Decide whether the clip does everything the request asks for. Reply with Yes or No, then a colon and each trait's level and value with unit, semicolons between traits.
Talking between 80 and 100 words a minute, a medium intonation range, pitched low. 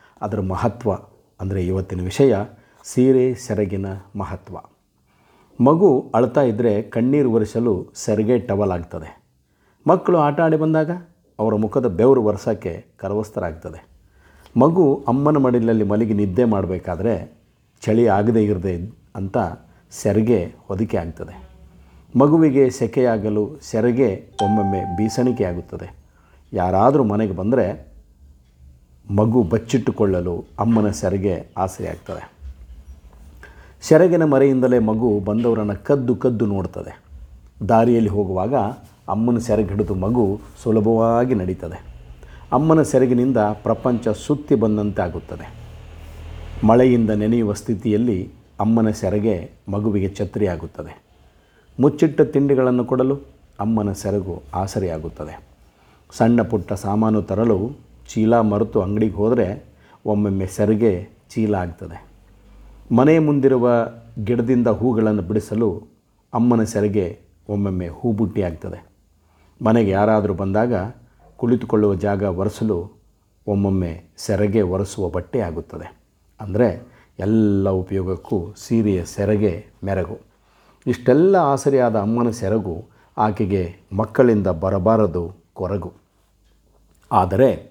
Yes: average, 90 wpm; average, 3.7 semitones; low, 105 Hz